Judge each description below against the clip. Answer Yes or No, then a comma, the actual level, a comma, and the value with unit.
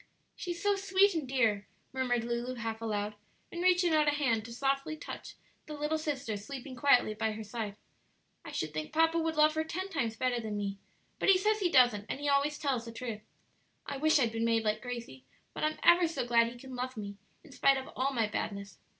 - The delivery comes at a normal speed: No, fast, 220 wpm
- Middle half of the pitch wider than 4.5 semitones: Yes, wide, 5.4 semitones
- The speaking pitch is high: Yes, very high, 255 Hz